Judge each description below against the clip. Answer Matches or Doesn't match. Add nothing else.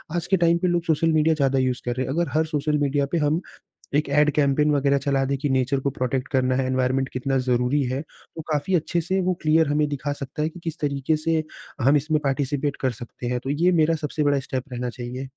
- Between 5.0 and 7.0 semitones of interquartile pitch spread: Doesn't match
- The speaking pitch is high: Doesn't match